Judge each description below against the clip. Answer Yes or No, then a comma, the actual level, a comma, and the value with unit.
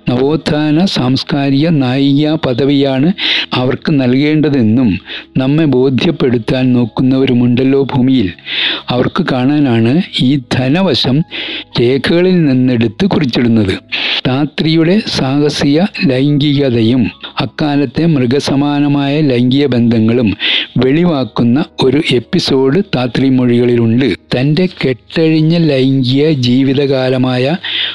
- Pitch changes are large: No, average, 3.0 semitones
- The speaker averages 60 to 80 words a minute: Yes, average, 75 wpm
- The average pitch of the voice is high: No, low, 135 Hz